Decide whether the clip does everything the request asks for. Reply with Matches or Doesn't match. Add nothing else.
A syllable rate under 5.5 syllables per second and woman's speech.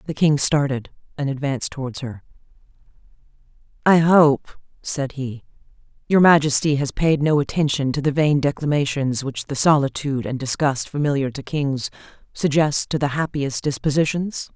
Matches